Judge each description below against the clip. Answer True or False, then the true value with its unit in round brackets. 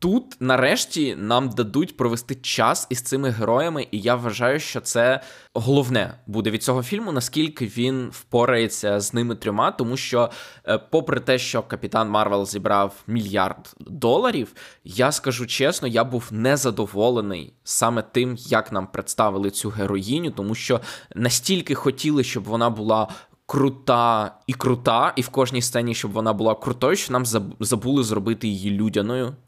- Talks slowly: False (145 wpm)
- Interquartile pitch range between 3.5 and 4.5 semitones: False (3.0 semitones)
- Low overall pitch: True (120 Hz)